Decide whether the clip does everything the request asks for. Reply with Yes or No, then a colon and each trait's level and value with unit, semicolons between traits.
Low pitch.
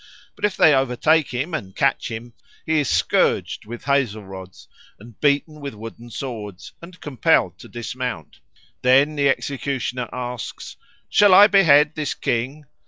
Yes: low, 130 Hz